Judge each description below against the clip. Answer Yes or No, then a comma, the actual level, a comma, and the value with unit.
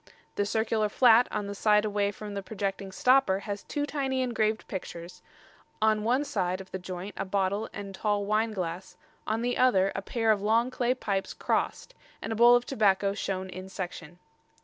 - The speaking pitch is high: Yes, high, 205 Hz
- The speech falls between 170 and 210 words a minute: Yes, average, 190 wpm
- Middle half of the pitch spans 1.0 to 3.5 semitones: Yes, average, 2.8 semitones